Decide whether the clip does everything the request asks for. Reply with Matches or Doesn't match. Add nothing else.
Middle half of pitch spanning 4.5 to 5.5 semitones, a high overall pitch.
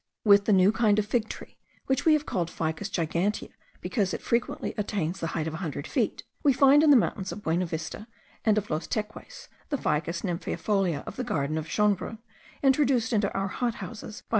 Matches